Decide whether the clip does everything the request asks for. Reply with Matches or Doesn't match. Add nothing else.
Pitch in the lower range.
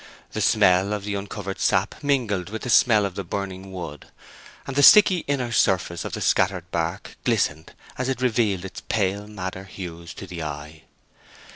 Matches